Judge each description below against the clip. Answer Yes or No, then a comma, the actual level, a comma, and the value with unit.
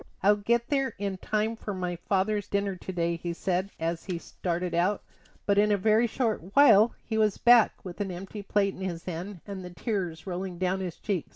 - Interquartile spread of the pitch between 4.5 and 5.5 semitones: No, average, 2.9 semitones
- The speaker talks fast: Yes, fast, 210 wpm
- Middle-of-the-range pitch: No, high, 195 Hz